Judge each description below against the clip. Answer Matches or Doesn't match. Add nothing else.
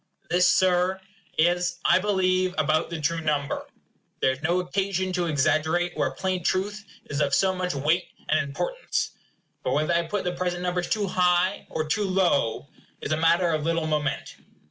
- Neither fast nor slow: Matches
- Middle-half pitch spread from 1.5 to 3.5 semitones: Matches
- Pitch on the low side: Doesn't match